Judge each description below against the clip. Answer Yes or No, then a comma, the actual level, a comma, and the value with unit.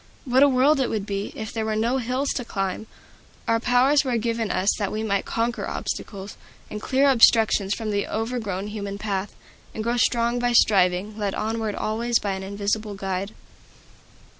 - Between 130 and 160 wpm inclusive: No, average, 180 wpm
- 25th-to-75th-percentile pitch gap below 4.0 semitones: Yes, average, 3.1 semitones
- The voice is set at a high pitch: Yes, high, 220 Hz